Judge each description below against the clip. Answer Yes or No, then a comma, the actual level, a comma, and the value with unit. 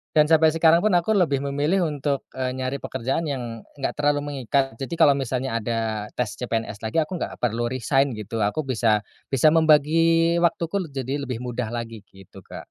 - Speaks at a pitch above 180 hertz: No, low, 135 Hz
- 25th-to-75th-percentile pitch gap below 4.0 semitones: No, average, 4.9 semitones